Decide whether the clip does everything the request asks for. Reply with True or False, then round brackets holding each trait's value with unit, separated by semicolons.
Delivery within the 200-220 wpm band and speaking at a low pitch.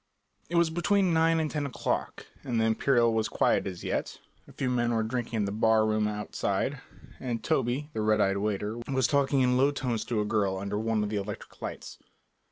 True (205 wpm; 115 Hz)